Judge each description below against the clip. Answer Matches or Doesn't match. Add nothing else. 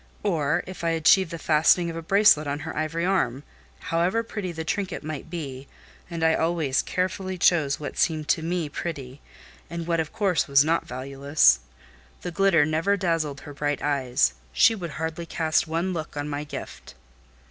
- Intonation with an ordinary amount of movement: Matches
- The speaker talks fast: Doesn't match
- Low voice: Doesn't match